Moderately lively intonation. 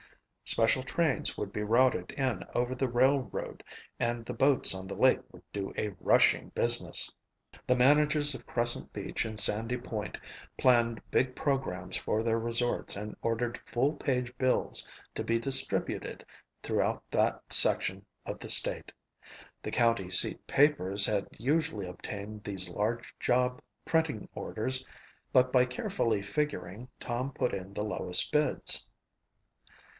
Yes: average, 3.6 semitones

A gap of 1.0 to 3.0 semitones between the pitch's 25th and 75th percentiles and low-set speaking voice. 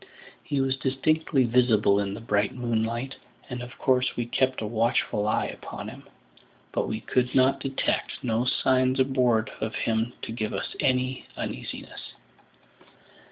Yes: average, 2.7 semitones; low, 120 Hz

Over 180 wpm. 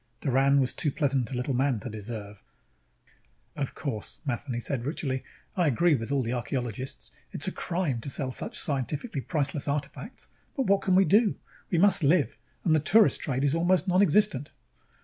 No: average, 175 wpm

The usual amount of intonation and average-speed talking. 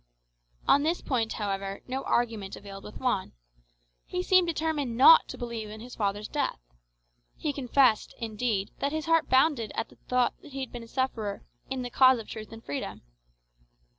Yes: average, 4.3 semitones; average, 180 wpm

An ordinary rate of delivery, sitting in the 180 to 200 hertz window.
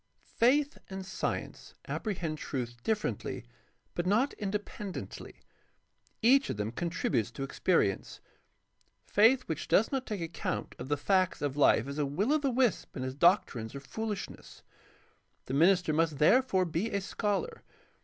Yes: average, 150 wpm; medium, 185 Hz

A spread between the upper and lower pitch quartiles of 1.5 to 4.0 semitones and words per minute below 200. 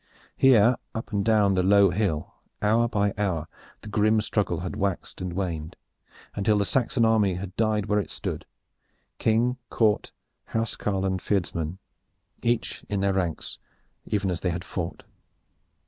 Yes: average, 2.9 semitones; average, 155 wpm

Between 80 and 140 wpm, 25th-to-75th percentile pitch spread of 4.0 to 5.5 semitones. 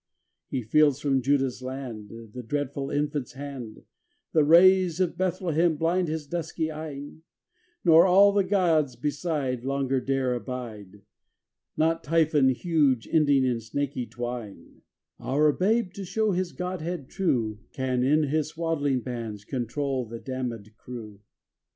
Yes: slow, 135 wpm; average, 4.6 semitones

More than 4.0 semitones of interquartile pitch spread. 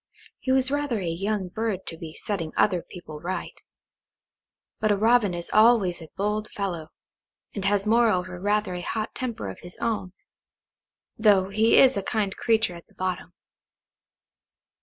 No: average, 3.6 semitones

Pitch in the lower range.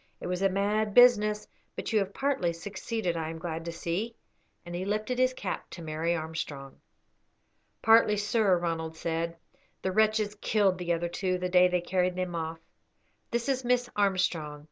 No: medium, 185 Hz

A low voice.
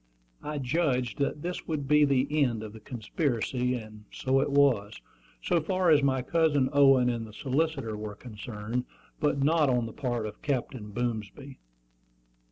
Yes: low, 130 Hz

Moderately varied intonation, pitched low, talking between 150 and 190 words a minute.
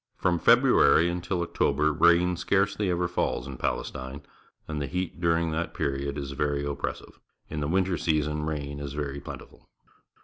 Yes: average, 3.4 semitones; very low, 75 Hz; average, 160 wpm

